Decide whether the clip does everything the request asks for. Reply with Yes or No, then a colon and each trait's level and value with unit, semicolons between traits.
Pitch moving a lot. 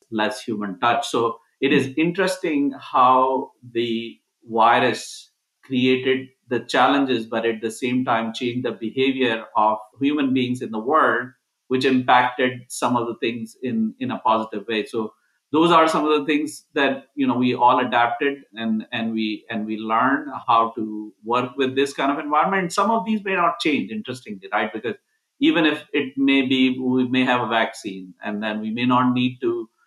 No: average, 4.0 semitones